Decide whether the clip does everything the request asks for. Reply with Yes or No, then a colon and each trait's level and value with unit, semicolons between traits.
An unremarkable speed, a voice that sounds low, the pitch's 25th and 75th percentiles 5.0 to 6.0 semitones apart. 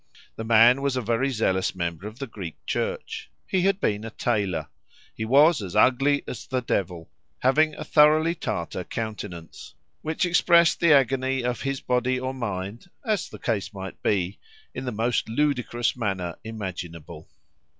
Yes: average, 160 wpm; low, 120 Hz; wide, 5.6 semitones